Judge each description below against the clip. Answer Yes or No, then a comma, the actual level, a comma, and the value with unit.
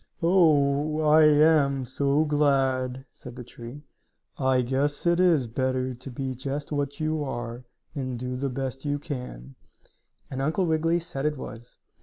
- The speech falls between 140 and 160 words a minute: Yes, average, 155 wpm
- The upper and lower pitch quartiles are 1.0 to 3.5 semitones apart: Yes, average, 2.9 semitones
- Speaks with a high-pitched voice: No, medium, 140 Hz